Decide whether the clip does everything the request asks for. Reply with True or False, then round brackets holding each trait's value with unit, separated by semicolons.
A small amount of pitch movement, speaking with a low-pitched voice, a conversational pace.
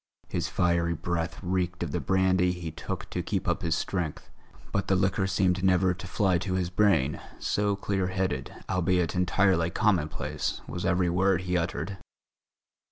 True (1.7 semitones; 90 Hz; 165 wpm)